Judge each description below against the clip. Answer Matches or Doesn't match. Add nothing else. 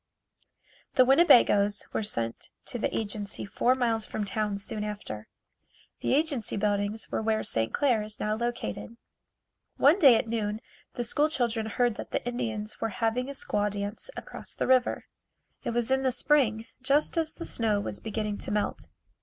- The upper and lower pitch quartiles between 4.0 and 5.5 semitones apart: Doesn't match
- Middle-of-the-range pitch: Doesn't match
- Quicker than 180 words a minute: Doesn't match